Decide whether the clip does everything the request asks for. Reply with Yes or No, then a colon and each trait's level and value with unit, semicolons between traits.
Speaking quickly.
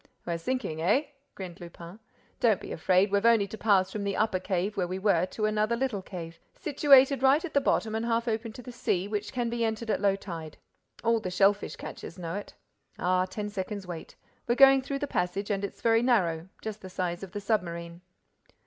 Yes: fast, 210 wpm